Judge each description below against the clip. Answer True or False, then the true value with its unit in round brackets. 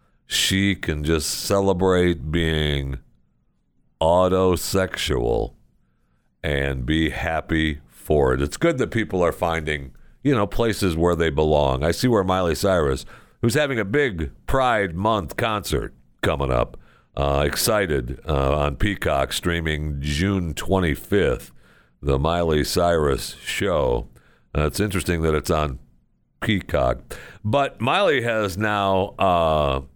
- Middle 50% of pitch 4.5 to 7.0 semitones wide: True (5.1 semitones)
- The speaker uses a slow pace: True (120 wpm)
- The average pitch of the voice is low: True (80 Hz)